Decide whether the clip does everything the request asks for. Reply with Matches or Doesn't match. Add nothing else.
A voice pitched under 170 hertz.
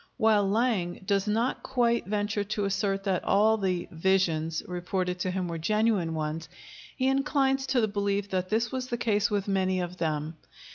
Doesn't match